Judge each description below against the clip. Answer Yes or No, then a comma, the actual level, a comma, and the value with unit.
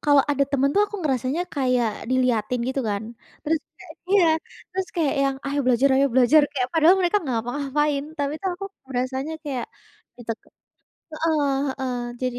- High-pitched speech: Yes, very high, 275 Hz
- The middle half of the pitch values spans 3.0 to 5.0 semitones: Yes, average, 3.3 semitones